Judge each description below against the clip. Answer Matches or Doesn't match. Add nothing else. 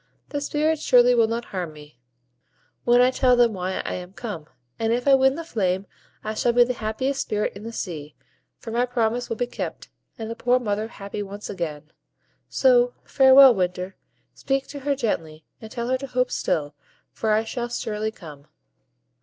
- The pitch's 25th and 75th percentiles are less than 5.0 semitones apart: Matches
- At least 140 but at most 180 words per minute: Doesn't match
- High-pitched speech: Matches